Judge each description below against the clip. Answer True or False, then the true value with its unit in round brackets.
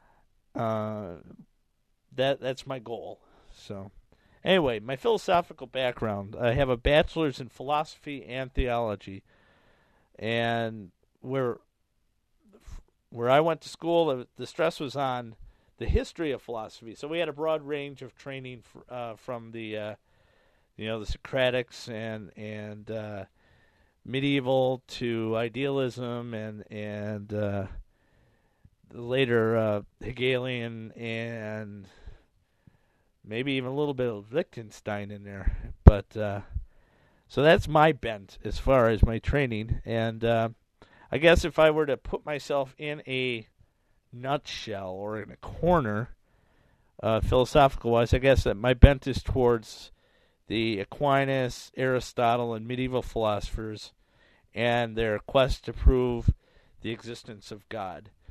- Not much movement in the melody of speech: False (3.8 semitones)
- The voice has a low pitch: True (115 Hz)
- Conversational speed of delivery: False (130 wpm)